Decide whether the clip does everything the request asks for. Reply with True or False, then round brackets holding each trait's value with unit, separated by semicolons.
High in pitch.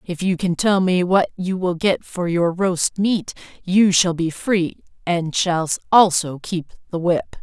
False (175 Hz)